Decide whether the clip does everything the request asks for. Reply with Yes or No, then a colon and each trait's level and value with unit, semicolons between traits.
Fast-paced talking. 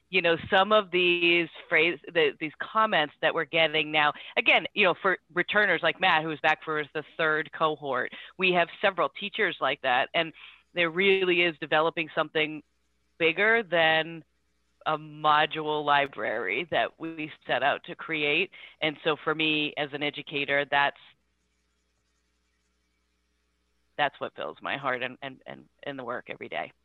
No: average, 155 wpm